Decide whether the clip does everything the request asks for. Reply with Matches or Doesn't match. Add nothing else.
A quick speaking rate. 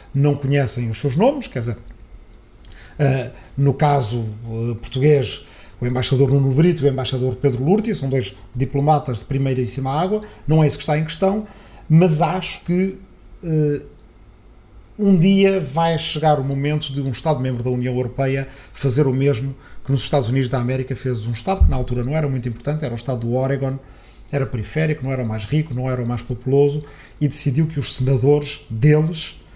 Matches